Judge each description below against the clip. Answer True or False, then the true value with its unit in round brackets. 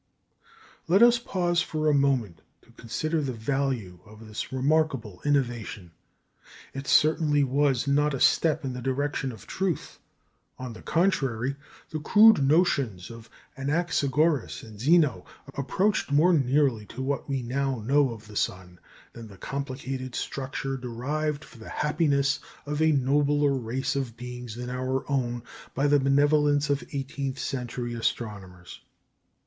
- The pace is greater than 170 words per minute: False (145 wpm)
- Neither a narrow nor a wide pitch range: True (3.5 semitones)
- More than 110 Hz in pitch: True (135 Hz)